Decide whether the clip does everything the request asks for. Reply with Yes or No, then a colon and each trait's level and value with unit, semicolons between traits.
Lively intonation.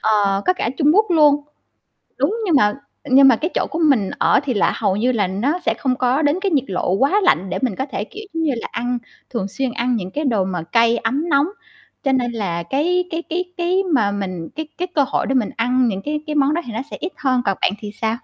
Yes: wide, 6.4 semitones